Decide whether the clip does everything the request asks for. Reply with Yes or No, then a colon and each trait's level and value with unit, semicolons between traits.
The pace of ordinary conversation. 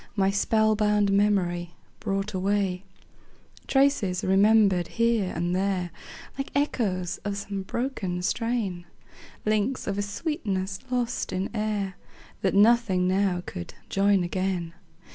No: slow, 120 wpm